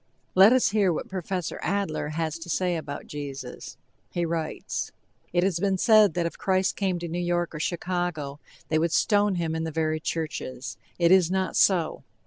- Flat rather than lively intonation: No, average, 3.0 semitones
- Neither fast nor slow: Yes, average, 185 wpm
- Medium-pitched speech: Yes, medium, 170 Hz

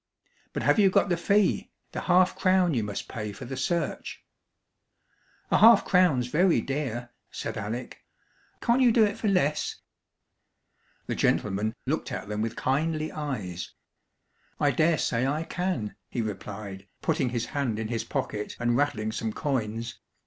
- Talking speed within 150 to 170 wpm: Yes, average, 155 wpm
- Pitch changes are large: Yes, wide, 7.7 semitones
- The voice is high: No, low, 135 Hz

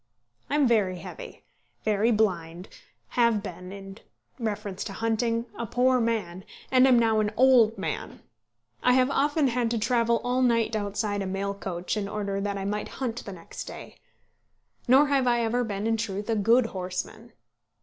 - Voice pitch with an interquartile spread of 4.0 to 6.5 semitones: No, average, 3.2 semitones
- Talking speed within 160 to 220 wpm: Yes, average, 175 wpm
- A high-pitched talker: Yes, high, 220 Hz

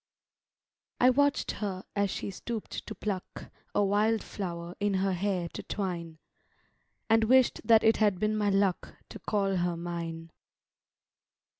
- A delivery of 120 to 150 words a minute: Yes, average, 140 wpm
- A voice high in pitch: Yes, high, 200 Hz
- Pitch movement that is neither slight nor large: Yes, average, 3.3 semitones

